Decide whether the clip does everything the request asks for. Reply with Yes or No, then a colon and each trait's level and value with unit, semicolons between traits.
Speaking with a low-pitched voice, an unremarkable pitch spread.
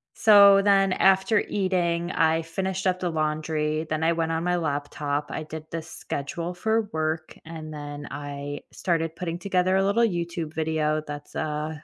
No: medium, 165 Hz; average, 3.1 semitones